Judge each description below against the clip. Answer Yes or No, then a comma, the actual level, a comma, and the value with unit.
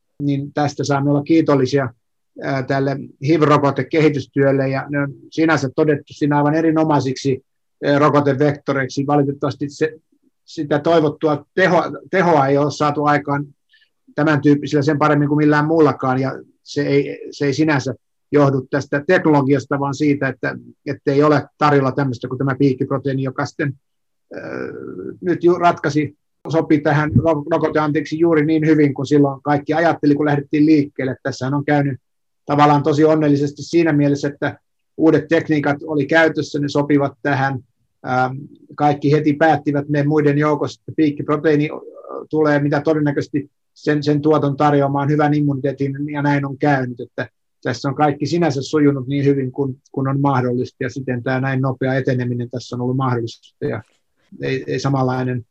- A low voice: No, medium, 145 Hz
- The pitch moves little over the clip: Yes, narrow, 1.8 semitones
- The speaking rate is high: No, average, 145 wpm